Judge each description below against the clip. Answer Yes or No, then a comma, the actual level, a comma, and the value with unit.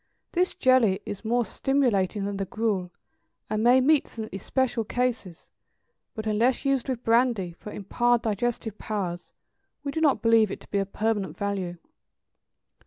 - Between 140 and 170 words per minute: Yes, average, 155 wpm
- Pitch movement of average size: Yes, average, 3.9 semitones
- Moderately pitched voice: No, high, 225 Hz